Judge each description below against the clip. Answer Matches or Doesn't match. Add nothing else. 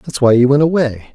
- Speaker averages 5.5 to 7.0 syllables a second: Matches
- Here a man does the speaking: Matches